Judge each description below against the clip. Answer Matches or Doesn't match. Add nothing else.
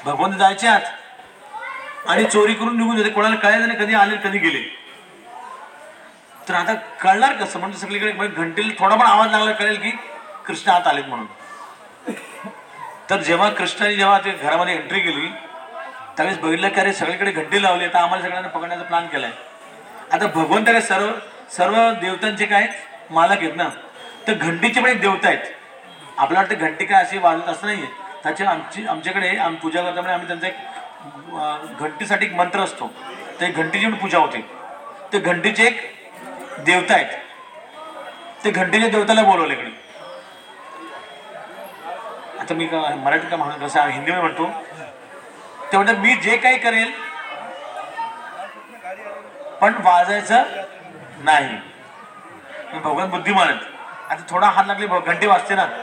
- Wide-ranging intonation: Doesn't match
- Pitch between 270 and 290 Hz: Doesn't match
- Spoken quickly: Matches